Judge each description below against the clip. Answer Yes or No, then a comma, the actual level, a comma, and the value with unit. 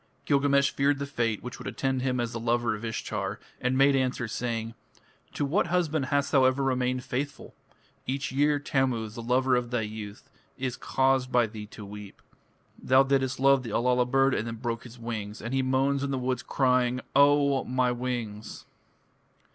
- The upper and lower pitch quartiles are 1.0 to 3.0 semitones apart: Yes, narrow, 2.6 semitones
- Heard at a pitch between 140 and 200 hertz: No, low, 130 Hz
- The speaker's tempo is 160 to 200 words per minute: Yes, average, 185 wpm